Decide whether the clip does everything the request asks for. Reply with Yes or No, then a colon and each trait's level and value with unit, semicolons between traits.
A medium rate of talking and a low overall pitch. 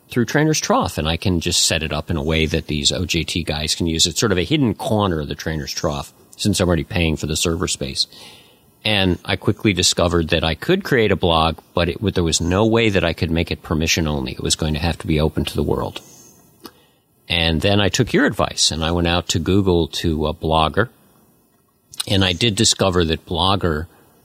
No: fast, 230 wpm; very low, 85 Hz